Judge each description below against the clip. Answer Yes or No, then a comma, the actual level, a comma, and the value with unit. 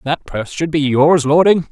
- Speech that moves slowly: No, fast, 210 wpm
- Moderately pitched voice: Yes, medium, 150 Hz